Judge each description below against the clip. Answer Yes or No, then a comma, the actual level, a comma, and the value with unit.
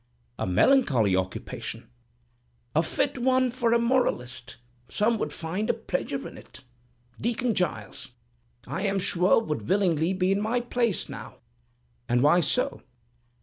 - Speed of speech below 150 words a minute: Yes, average, 140 wpm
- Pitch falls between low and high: No, high, 195 Hz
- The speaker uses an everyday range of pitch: No, wide, 7.8 semitones